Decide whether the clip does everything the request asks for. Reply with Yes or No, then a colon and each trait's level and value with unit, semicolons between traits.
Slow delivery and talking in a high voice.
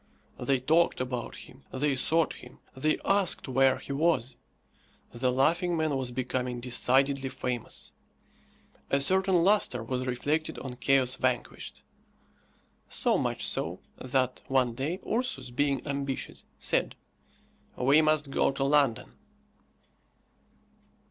No: slow, 120 wpm; low, 135 Hz